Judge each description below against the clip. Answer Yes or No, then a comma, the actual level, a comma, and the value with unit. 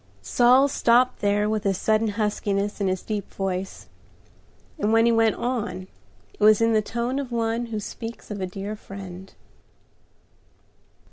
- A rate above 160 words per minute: No, average, 155 wpm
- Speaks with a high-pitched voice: Yes, high, 215 Hz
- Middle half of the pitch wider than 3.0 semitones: No, average, 2.7 semitones